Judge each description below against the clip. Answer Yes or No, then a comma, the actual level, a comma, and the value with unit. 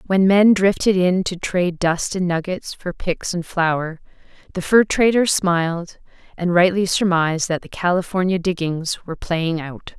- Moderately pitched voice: Yes, medium, 180 Hz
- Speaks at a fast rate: No, average, 160 wpm